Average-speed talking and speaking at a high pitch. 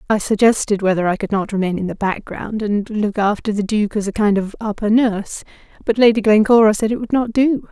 No: fast, 220 wpm; high, 210 Hz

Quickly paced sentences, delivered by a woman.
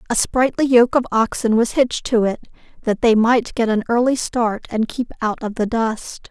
Yes: fast, 210 wpm; female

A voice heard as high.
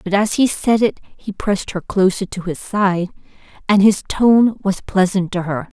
Yes: high, 195 Hz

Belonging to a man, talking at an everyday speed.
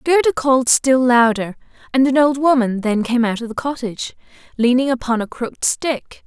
No: female; average, 180 wpm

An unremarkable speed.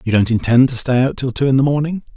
No: fast, 305 wpm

